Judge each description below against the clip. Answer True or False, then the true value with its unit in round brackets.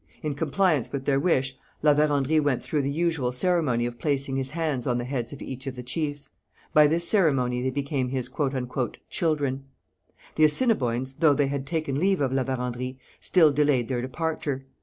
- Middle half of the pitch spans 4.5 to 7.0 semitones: False (3.0 semitones)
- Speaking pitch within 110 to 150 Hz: True (140 Hz)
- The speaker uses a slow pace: False (180 wpm)